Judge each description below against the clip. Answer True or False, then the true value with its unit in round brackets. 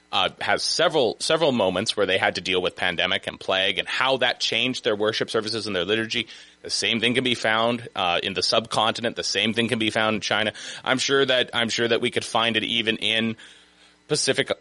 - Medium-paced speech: False (235 wpm)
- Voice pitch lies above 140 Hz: False (110 Hz)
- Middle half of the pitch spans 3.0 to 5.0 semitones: False (2.6 semitones)